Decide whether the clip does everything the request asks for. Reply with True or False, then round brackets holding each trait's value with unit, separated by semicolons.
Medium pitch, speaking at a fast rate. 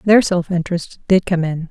True (175 Hz; 210 wpm)